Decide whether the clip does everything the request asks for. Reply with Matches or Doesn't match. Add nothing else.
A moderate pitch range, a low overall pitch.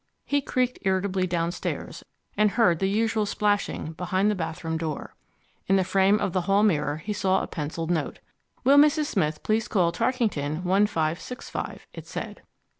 Doesn't match